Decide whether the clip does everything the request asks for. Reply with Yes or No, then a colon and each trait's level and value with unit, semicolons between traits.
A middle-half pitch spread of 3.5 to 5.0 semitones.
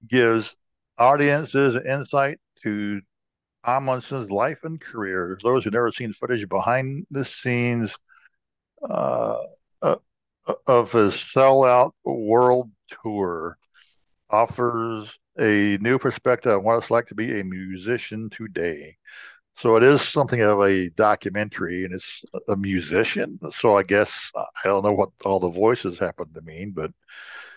Yes: average, 4.0 semitones